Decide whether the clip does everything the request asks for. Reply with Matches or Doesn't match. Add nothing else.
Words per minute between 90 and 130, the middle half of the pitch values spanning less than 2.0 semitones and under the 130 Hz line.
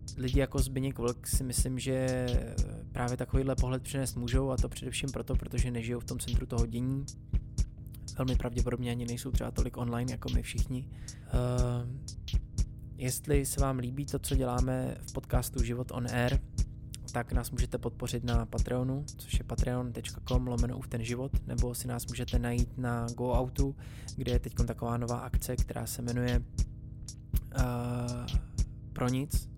Doesn't match